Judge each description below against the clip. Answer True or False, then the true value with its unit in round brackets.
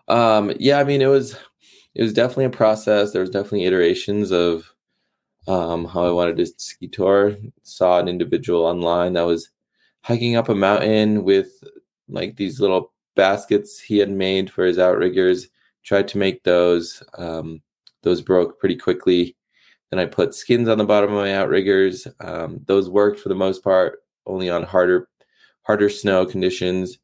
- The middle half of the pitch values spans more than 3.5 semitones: False (3.2 semitones)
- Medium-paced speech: True (170 wpm)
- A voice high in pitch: False (95 Hz)